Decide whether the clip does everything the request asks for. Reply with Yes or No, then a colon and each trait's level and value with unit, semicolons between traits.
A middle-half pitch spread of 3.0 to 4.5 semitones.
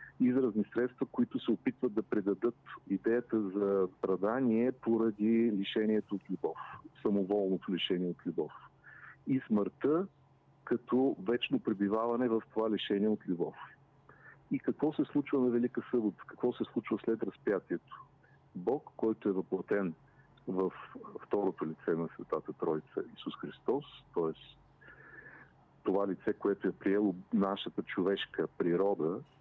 Yes: average, 3.5 semitones